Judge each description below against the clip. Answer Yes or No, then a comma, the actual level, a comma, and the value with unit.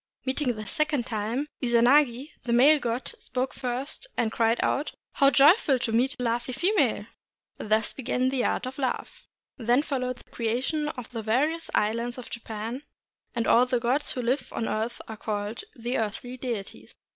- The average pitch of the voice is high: Yes, high, 245 Hz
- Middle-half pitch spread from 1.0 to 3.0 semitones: Yes, average, 2.7 semitones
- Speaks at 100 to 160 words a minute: No, average, 180 wpm